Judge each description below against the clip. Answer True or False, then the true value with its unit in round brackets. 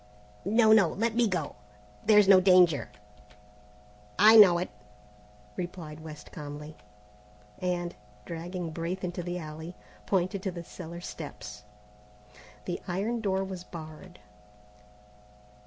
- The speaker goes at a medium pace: False (115 wpm)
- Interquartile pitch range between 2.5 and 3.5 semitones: True (2.8 semitones)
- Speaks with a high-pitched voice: False (175 Hz)